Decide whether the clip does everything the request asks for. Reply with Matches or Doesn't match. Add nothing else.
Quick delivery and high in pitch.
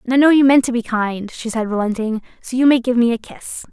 Matches